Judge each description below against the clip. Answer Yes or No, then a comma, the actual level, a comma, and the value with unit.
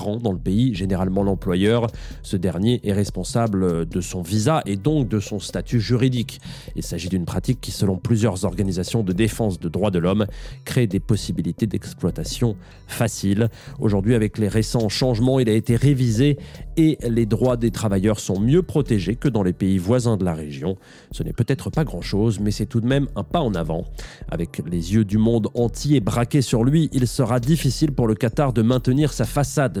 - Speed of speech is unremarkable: Yes, average, 190 wpm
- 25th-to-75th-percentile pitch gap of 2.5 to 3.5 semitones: No, average, 4.4 semitones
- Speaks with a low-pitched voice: Yes, low, 115 Hz